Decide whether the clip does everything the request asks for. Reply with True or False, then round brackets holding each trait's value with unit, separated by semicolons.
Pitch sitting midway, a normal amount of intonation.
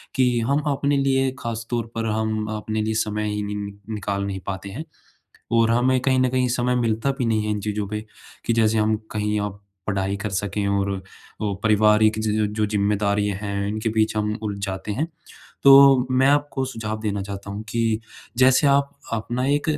False (110 Hz; 3.3 semitones)